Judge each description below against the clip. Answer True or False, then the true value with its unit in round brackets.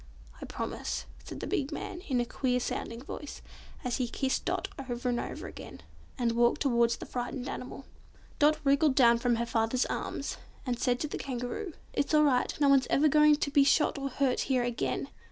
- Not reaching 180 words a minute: False (200 wpm)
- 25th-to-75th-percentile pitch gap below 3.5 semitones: True (2.8 semitones)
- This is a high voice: True (260 Hz)